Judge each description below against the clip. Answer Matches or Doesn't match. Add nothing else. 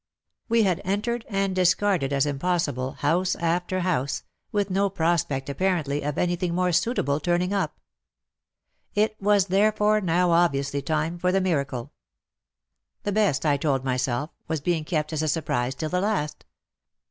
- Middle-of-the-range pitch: Matches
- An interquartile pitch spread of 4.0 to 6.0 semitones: Matches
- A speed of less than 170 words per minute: Matches